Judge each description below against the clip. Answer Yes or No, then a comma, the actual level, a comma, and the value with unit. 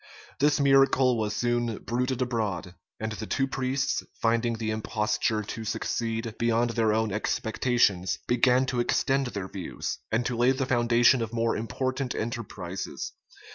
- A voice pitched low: Yes, low, 115 Hz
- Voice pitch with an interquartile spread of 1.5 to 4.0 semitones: Yes, narrow, 2.5 semitones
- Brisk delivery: No, average, 150 wpm